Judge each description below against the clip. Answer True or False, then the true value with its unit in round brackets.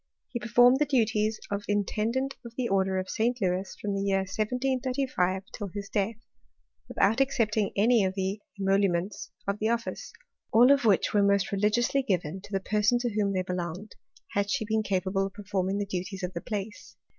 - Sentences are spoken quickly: False (180 wpm)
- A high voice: True (205 Hz)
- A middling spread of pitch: True (3.1 semitones)